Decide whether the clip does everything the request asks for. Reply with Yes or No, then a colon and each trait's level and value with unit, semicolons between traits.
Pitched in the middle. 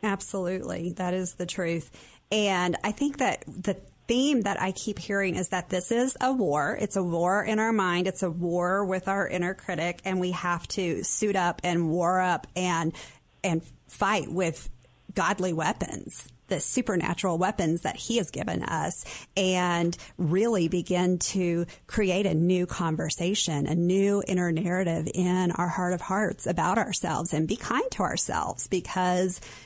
Yes: medium, 180 Hz